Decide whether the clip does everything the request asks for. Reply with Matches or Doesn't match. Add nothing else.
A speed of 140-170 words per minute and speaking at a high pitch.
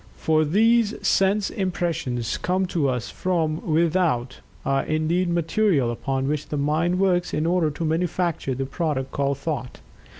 Doesn't match